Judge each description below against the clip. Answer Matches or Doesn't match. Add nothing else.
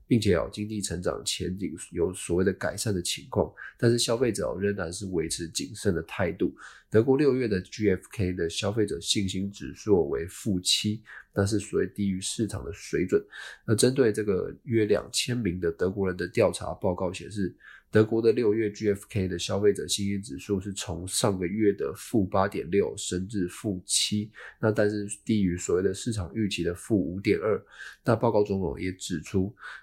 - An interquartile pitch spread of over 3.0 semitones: Doesn't match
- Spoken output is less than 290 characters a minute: Matches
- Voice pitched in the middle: Doesn't match